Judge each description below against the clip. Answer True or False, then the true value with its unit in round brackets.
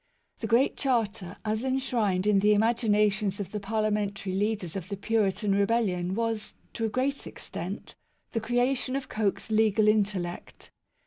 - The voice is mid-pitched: False (215 Hz)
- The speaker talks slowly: False (145 wpm)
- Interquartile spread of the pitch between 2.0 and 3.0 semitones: True (2.4 semitones)